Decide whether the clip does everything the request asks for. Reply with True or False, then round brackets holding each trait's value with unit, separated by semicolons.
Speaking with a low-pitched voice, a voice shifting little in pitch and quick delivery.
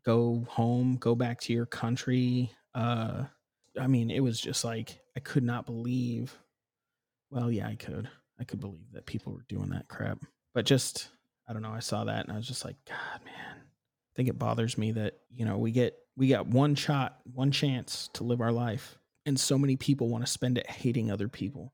True (120 Hz; 2.0 semitones; 215 wpm)